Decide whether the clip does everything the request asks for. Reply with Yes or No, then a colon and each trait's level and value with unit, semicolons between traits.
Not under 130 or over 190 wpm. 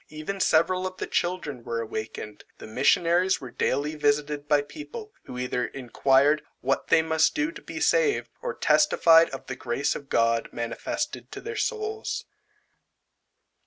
Yes: average, 155 wpm